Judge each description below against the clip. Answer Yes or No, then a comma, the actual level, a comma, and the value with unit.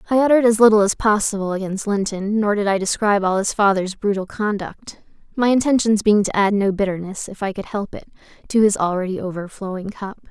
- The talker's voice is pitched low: No, high, 205 Hz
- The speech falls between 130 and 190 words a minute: No, average, 200 wpm